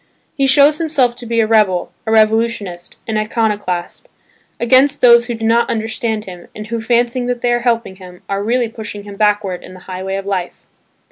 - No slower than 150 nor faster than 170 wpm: No, average, 195 wpm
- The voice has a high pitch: Yes, high, 220 Hz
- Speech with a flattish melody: No, average, 3.1 semitones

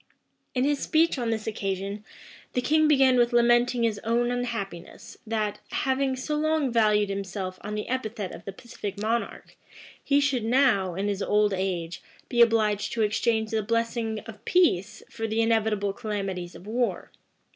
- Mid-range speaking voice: No, high, 225 Hz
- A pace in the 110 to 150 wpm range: No, average, 165 wpm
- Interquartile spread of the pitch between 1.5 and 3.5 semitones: Yes, average, 3.2 semitones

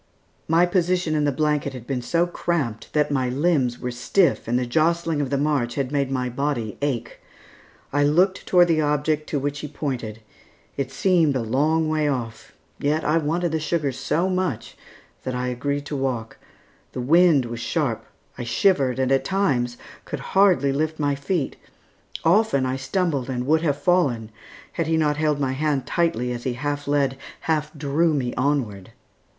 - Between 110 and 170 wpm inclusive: No, average, 180 wpm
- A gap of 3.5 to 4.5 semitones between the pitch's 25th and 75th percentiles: Yes, average, 3.8 semitones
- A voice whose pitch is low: No, medium, 145 Hz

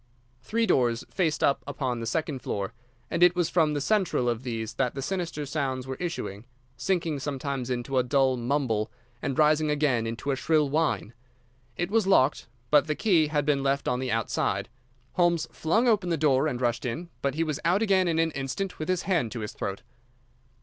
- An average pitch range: Yes, average, 4.7 semitones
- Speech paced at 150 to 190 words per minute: No, average, 200 wpm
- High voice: No, medium, 145 Hz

